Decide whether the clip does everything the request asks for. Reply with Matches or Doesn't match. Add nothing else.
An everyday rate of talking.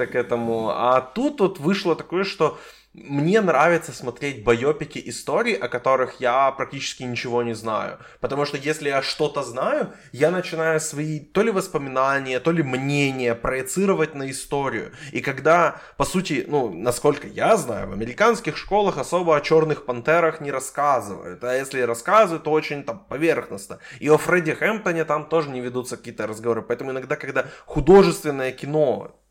Doesn't match